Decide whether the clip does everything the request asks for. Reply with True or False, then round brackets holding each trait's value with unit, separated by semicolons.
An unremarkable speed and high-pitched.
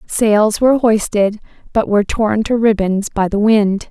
True (170 wpm; 215 Hz)